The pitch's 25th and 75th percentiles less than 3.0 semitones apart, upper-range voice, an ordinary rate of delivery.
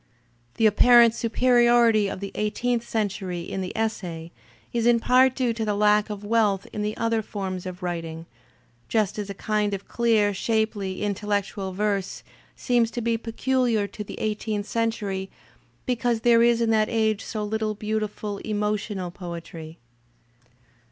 Yes: narrow, 2.5 semitones; high, 215 Hz; average, 155 wpm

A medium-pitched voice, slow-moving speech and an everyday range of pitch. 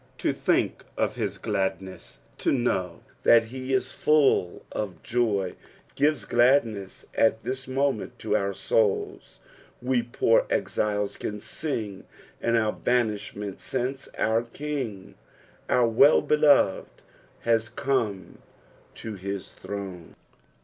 No: low, 115 Hz; slow, 115 wpm; average, 4.4 semitones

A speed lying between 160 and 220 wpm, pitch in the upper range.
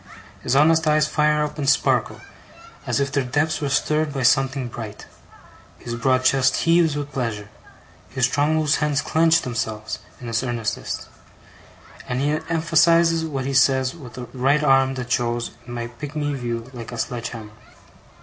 No: average, 170 wpm; low, 135 Hz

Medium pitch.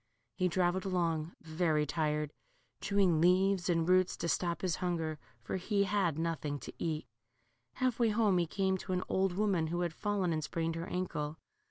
Yes: medium, 175 Hz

